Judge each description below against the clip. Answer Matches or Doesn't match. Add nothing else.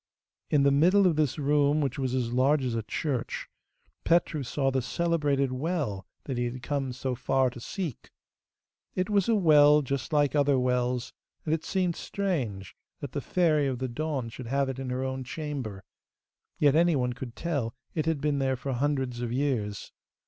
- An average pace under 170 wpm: Doesn't match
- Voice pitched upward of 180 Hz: Doesn't match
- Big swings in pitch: Doesn't match